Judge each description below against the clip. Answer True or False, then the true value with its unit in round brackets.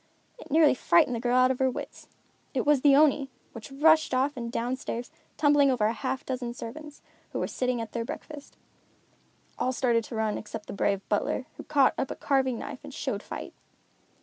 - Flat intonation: False (3.2 semitones)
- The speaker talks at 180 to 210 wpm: True (200 wpm)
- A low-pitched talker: False (255 Hz)